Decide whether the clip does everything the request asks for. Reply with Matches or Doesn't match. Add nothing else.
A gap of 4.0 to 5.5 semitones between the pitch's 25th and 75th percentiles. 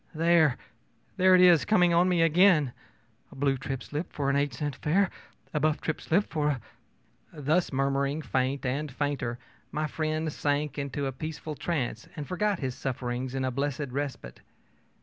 Doesn't match